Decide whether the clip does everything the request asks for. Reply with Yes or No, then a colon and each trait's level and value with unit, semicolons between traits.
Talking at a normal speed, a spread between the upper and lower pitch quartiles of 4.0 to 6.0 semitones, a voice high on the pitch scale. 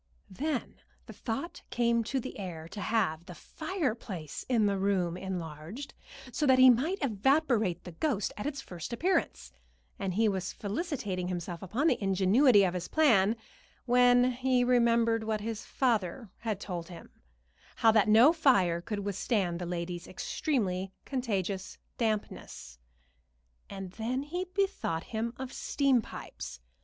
Yes: average, 145 wpm; wide, 5.6 semitones; high, 220 Hz